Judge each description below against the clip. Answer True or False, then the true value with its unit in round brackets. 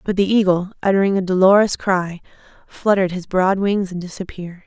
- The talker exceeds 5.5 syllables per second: True (5.8 syllables/s)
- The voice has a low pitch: False (190 Hz)